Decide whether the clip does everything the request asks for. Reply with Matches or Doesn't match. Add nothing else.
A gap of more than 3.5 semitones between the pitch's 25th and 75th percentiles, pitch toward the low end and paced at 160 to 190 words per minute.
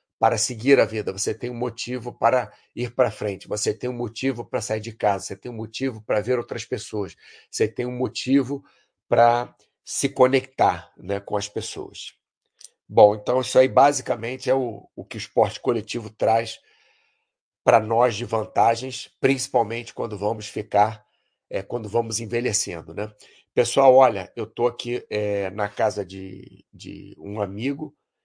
Doesn't match